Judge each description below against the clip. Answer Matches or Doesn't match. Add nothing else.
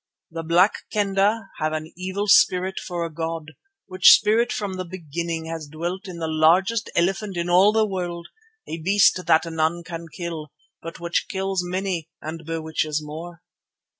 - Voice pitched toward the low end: Doesn't match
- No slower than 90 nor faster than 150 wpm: Doesn't match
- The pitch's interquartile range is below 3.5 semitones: Matches